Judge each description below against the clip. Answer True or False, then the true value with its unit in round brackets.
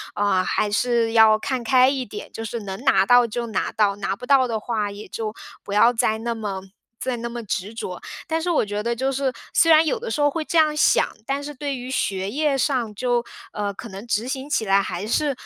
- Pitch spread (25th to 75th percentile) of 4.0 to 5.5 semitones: True (4.3 semitones)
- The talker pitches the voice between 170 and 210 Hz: False (235 Hz)